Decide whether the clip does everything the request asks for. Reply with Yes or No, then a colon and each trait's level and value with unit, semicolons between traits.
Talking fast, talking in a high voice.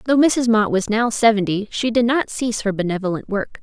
Yes: fast, 215 wpm; high, 220 Hz